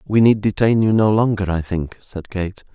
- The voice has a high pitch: No, low, 100 Hz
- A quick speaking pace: Yes, fast, 220 wpm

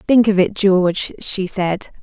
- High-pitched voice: Yes, high, 195 Hz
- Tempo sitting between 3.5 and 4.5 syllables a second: Yes, 4.1 syllables/s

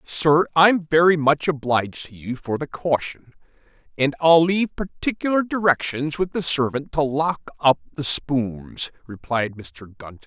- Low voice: No, medium, 145 Hz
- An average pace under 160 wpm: Yes, average, 150 wpm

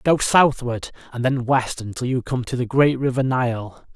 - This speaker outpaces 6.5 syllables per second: No, 4.5 syllables/s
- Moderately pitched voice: No, low, 125 Hz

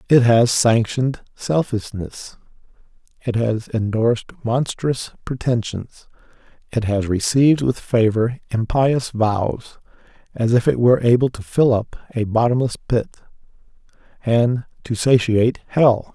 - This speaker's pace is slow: Yes, slow, 115 wpm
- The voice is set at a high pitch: No, low, 120 Hz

